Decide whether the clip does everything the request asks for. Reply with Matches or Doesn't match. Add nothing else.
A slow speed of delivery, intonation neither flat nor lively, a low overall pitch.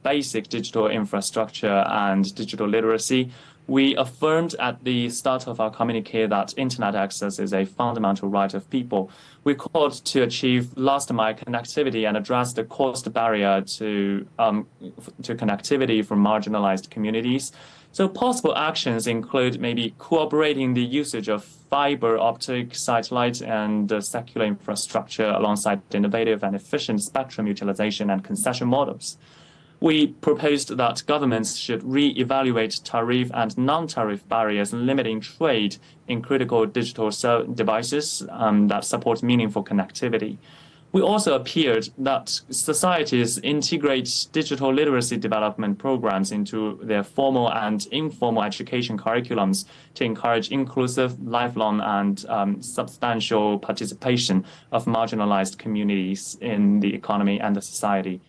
Matches